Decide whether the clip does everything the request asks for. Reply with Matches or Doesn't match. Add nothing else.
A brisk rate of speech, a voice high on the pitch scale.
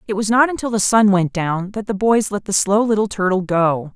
Matches